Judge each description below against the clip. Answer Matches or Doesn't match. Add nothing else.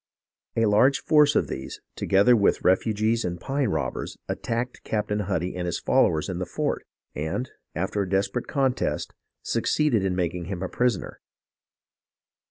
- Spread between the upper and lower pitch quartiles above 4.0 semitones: Matches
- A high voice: Doesn't match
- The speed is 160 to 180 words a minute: Doesn't match